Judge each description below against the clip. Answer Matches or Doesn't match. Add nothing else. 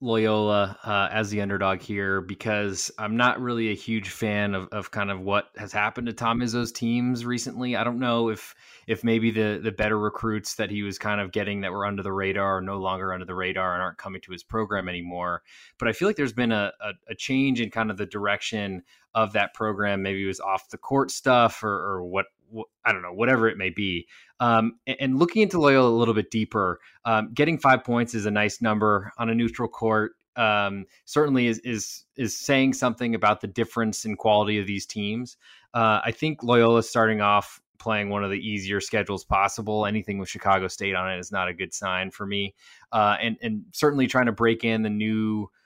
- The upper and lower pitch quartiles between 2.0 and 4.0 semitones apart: Matches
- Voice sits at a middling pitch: Doesn't match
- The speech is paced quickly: Matches